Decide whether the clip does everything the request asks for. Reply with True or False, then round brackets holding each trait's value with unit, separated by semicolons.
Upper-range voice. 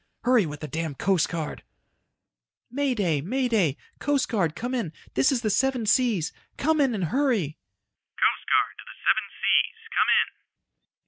True (215 Hz)